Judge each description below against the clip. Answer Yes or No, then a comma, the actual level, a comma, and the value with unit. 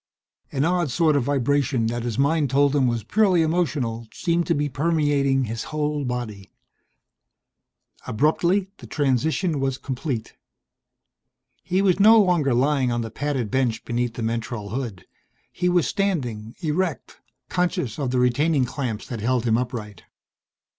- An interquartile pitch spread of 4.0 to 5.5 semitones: Yes, average, 5.0 semitones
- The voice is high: No, low, 135 Hz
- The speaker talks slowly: No, average, 145 wpm